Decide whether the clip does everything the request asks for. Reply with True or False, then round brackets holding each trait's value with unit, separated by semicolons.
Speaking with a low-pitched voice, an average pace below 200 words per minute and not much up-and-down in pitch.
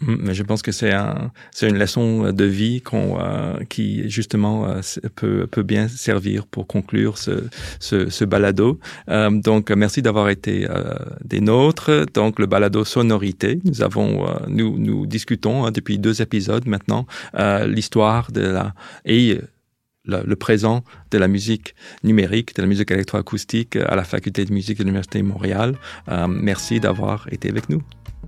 True (105 Hz; 170 wpm; 2.3 semitones)